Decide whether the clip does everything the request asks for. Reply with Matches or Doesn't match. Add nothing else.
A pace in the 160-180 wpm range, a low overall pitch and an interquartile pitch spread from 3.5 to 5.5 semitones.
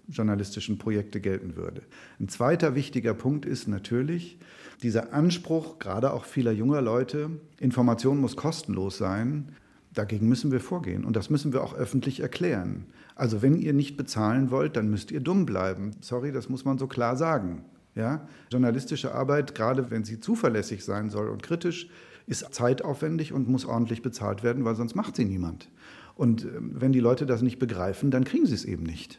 Matches